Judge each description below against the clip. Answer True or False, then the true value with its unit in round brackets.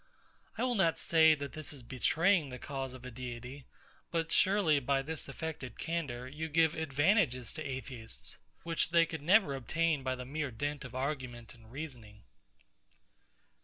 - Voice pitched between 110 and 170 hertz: True (140 Hz)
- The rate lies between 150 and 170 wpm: True (165 wpm)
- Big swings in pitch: False (4.1 semitones)